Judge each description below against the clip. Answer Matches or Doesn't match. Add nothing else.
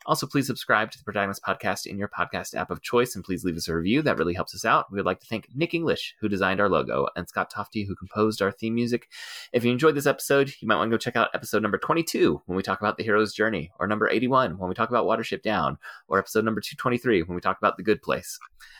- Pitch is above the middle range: Doesn't match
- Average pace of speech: Doesn't match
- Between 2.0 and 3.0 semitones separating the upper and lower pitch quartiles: Doesn't match